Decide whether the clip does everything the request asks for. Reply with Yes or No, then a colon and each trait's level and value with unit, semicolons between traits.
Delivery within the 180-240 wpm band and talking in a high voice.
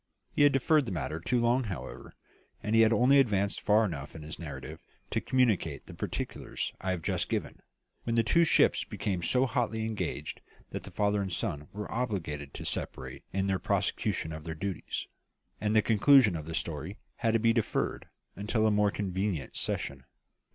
No: average, 185 wpm; low, 105 Hz